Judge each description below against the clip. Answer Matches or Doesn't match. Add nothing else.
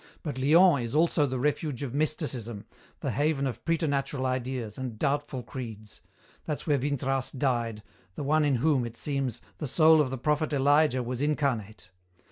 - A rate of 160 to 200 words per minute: Matches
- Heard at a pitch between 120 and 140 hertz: Matches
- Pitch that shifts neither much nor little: Matches